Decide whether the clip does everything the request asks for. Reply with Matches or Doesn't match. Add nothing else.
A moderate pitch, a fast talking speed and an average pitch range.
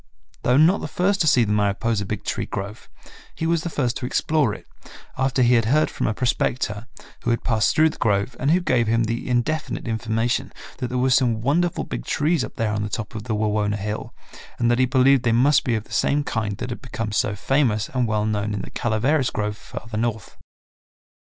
Doesn't match